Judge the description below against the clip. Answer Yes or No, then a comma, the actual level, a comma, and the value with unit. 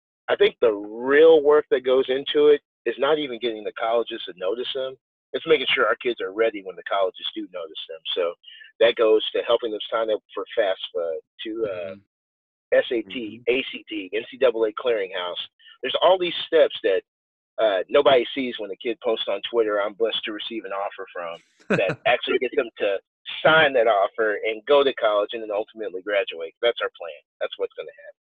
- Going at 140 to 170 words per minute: No, average, 195 wpm